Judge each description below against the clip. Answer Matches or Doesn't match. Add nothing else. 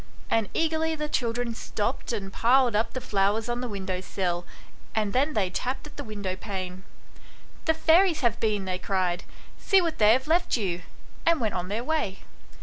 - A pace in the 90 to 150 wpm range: Doesn't match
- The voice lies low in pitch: Doesn't match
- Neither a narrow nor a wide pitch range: Doesn't match